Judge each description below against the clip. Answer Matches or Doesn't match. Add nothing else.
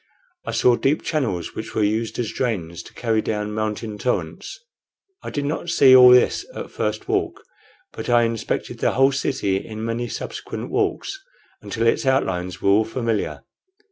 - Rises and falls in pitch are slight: Doesn't match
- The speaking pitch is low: Matches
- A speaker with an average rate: Matches